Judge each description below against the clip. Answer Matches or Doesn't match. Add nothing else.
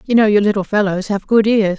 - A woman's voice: Matches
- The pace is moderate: Doesn't match